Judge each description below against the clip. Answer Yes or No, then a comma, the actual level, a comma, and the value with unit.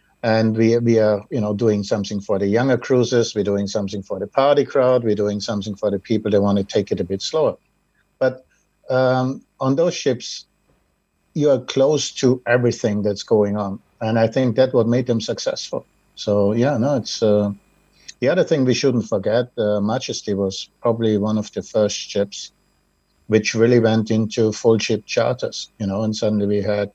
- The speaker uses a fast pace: No, average, 195 wpm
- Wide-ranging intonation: No, narrow, 2.6 semitones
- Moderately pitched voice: No, low, 110 Hz